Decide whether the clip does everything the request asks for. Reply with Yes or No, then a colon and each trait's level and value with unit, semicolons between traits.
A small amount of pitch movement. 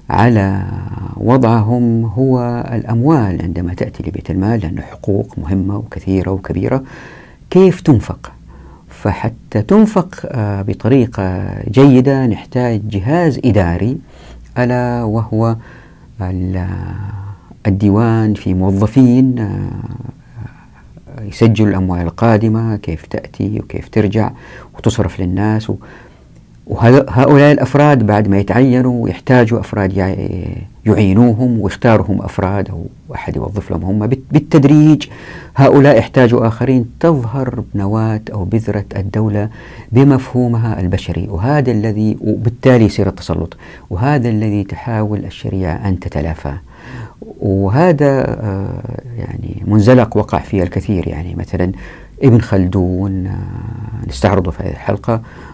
No: average, 4.2 semitones